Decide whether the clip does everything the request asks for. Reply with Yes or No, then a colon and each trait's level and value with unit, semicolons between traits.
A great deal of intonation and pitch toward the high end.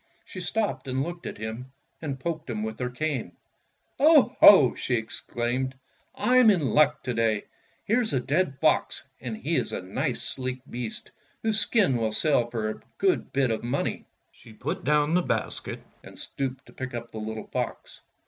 No: wide, 6.1 semitones; low, 130 Hz